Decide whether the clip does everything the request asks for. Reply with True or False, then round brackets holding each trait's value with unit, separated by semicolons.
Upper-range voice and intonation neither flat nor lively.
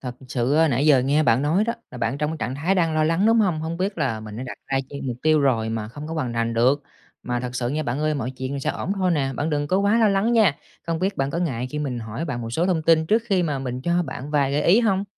False (150 Hz; 4.9 semitones)